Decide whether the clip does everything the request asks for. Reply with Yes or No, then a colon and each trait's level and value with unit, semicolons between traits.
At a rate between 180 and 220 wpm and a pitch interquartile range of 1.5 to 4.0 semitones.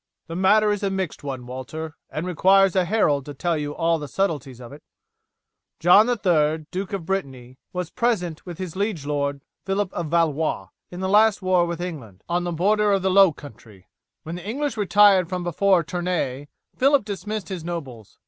No: average, 190 wpm; average, 4.6 semitones